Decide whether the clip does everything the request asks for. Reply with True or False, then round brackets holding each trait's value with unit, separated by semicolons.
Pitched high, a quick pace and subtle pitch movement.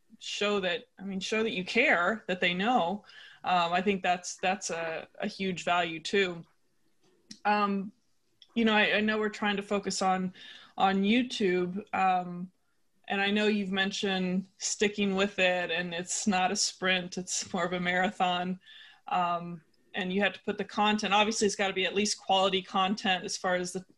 False (195 Hz; 185 wpm; 2.2 semitones)